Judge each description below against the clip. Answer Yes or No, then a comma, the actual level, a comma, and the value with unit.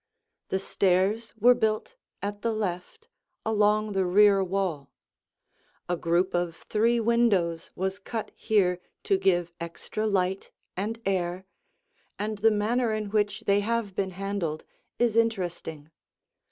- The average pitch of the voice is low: No, high, 200 Hz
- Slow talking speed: Yes, slow, 130 wpm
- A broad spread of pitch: No, average, 3.2 semitones